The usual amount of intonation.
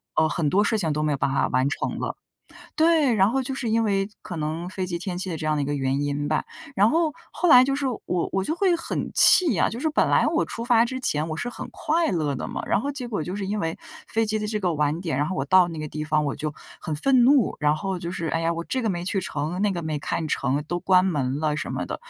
No: wide, 6.9 semitones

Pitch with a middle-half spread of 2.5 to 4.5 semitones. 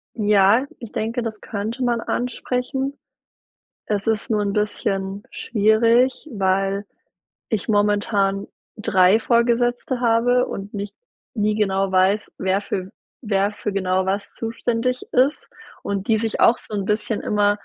Yes: average, 2.8 semitones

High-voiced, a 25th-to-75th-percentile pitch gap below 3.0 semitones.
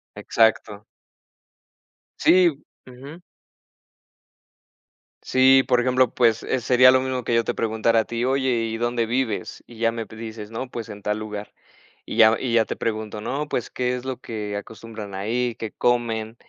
No: low, 115 Hz; narrow, 2.4 semitones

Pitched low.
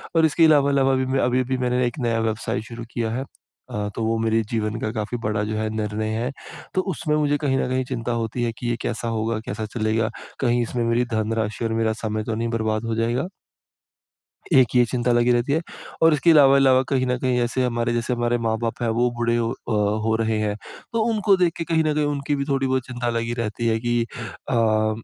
Yes: low, 120 Hz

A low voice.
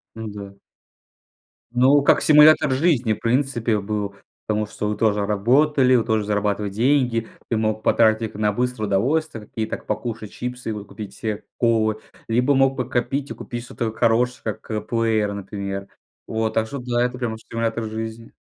Yes: low, 115 Hz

